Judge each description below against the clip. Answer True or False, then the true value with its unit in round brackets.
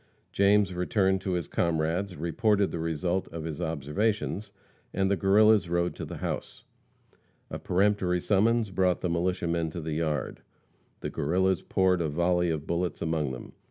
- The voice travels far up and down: False (2.8 semitones)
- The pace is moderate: True (160 wpm)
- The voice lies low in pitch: True (90 Hz)